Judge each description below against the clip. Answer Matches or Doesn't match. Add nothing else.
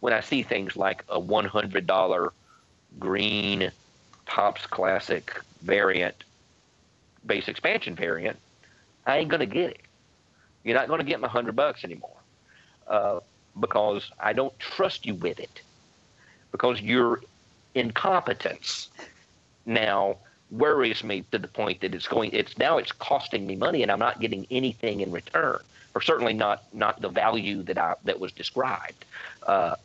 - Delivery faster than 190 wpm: Doesn't match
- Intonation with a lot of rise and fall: Doesn't match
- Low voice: Matches